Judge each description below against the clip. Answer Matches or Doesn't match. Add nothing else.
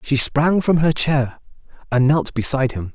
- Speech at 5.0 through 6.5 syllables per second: Doesn't match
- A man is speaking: Matches